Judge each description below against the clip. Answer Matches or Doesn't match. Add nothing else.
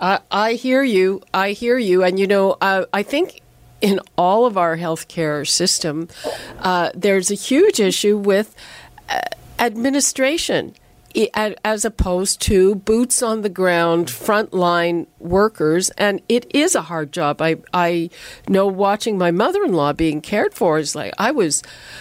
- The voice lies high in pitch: Matches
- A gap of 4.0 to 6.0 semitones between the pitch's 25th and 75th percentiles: Matches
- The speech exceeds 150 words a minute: Doesn't match